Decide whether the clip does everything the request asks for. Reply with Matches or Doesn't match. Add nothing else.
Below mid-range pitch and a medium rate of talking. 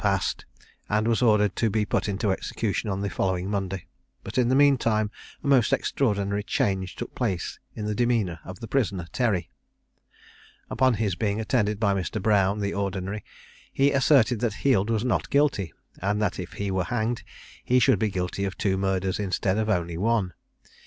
Matches